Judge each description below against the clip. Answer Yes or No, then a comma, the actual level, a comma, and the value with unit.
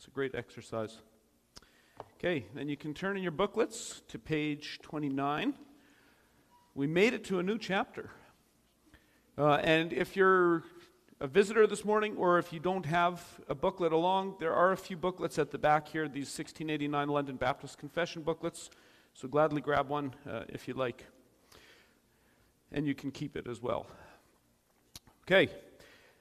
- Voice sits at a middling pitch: Yes, medium, 155 Hz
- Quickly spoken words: No, average, 160 wpm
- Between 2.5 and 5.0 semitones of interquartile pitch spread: Yes, average, 4.5 semitones